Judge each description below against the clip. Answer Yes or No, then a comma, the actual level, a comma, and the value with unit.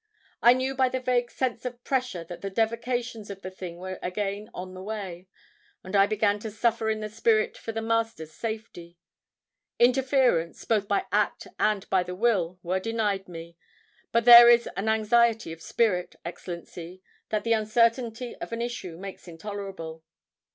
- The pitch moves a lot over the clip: No, average, 4.0 semitones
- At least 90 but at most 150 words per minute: No, average, 170 wpm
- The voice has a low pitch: No, high, 215 Hz